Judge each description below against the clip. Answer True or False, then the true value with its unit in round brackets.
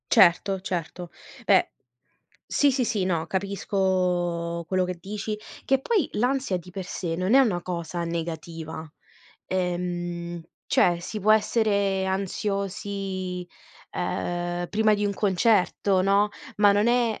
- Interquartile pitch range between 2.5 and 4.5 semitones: True (2.9 semitones)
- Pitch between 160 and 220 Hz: True (190 Hz)